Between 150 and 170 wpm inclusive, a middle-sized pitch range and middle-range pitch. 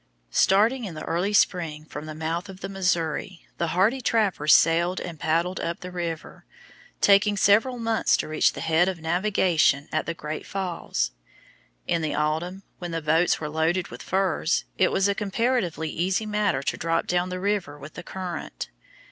No: average, 180 wpm; average, 3.4 semitones; medium, 175 Hz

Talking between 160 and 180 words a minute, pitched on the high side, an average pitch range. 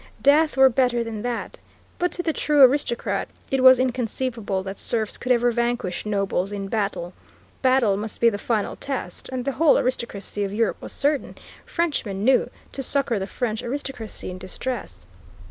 Yes: average, 170 wpm; high, 240 Hz; average, 4.3 semitones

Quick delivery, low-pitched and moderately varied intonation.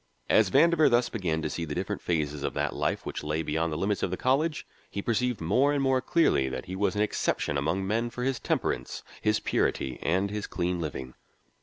No: fast, 215 wpm; very low, 95 Hz; wide, 7.3 semitones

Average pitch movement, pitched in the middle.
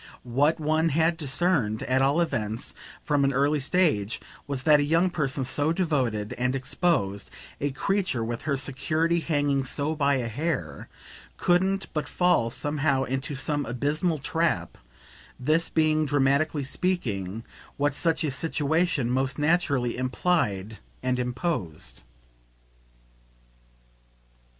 Yes: average, 4.0 semitones; medium, 145 Hz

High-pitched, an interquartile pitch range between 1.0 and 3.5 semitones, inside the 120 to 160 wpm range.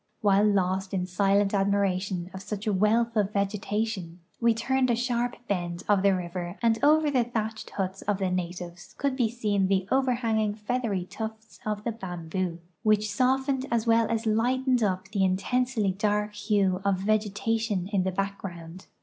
No: high, 205 Hz; average, 3.2 semitones; average, 175 wpm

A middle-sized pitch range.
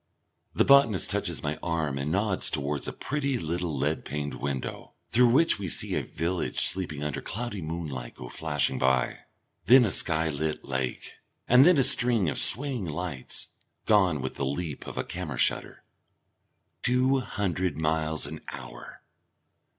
No: wide, 7.0 semitones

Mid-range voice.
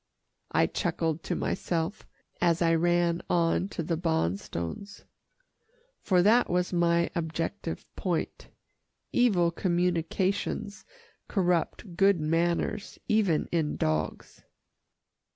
Yes: medium, 170 Hz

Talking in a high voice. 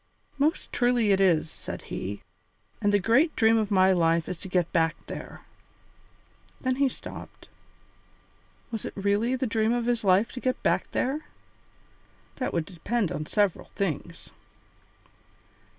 Yes: high, 205 Hz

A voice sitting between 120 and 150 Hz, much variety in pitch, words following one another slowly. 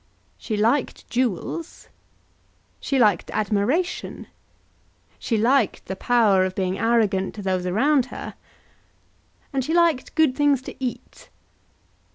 No: high, 235 Hz; wide, 5.7 semitones; slow, 120 wpm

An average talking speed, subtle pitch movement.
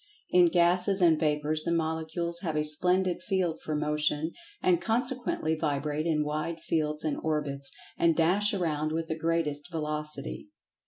Yes: average, 150 wpm; narrow, 2.2 semitones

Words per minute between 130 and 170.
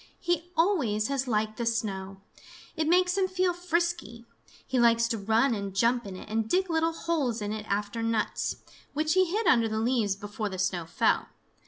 No: average, 190 wpm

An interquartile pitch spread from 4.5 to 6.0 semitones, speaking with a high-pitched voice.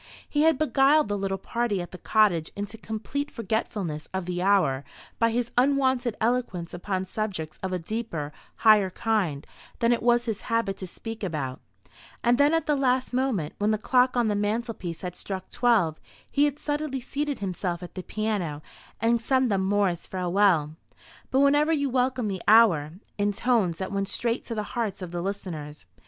Yes: average, 5.0 semitones; high, 215 Hz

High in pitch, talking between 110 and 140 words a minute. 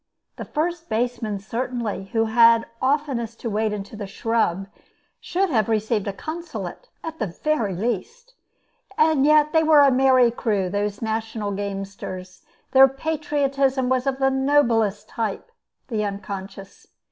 Yes: high, 230 Hz; slow, 135 wpm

